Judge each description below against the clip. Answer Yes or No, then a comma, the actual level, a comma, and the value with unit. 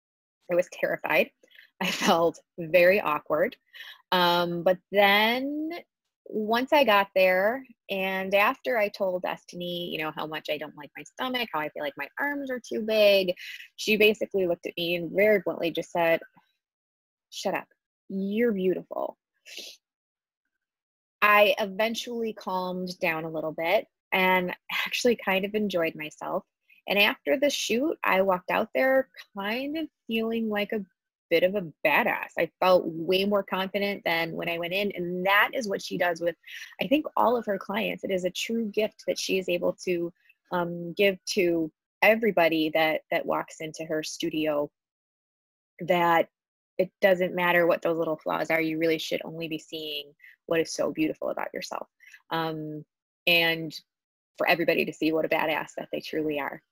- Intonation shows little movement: No, average, 4.0 semitones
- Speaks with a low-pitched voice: No, medium, 185 Hz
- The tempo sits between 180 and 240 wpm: No, average, 165 wpm